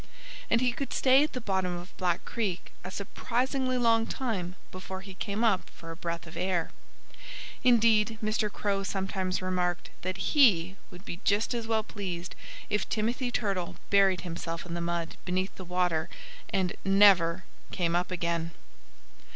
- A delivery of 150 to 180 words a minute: Yes, average, 160 wpm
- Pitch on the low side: No, high, 190 Hz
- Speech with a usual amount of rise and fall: Yes, average, 3.9 semitones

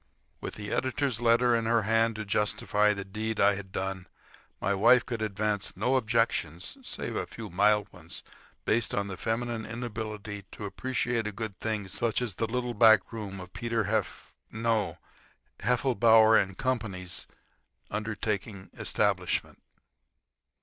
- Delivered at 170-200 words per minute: No, average, 145 wpm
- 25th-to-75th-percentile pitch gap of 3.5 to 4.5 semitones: No, narrow, 2.4 semitones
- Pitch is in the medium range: No, low, 110 Hz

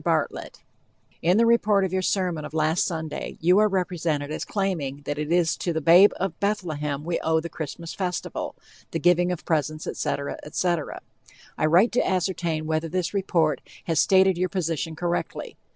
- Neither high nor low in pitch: Yes, medium, 170 Hz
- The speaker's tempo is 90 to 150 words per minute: No, average, 175 wpm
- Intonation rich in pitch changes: No, average, 2.9 semitones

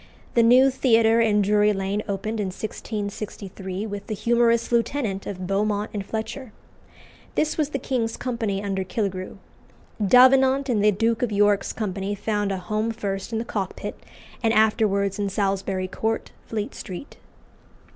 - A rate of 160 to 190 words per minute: No, average, 150 wpm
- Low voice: No, high, 210 Hz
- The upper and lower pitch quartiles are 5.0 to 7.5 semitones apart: No, narrow, 2.6 semitones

